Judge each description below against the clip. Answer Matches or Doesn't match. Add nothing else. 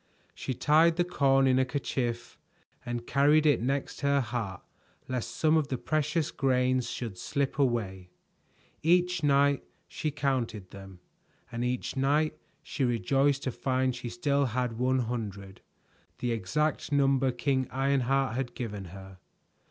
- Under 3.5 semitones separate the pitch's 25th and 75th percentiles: Matches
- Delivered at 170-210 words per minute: Doesn't match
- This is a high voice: Doesn't match